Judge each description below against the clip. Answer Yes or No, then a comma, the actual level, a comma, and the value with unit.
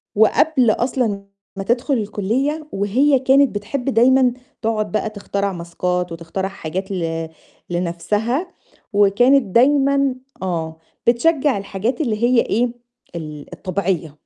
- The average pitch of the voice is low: No, high, 215 Hz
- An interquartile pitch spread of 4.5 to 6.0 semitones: Yes, wide, 5.5 semitones